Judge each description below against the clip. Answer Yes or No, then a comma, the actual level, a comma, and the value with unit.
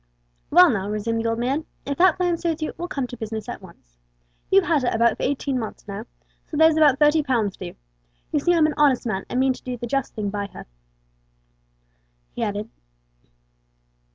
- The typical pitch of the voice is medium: No, very high, 255 Hz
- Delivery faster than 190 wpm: Yes, average, 200 wpm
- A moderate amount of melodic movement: No, wide, 5.9 semitones